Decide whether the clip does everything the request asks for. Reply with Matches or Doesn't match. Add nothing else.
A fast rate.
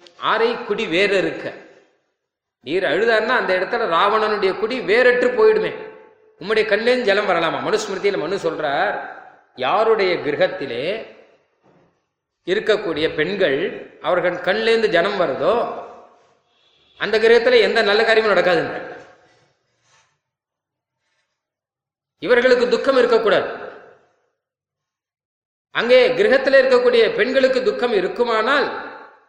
Doesn't match